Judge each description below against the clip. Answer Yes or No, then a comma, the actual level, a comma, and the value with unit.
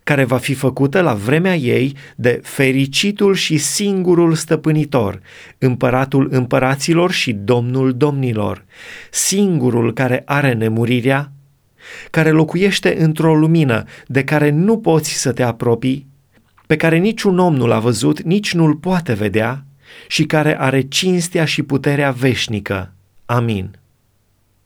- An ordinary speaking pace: Yes, average, 125 wpm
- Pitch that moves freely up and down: No, average, 4.6 semitones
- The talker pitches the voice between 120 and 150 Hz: Yes, low, 135 Hz